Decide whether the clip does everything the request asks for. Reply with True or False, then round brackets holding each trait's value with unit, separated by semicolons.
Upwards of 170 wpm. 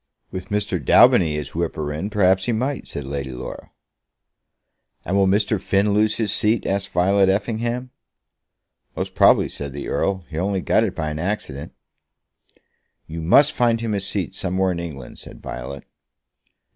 False (160 wpm)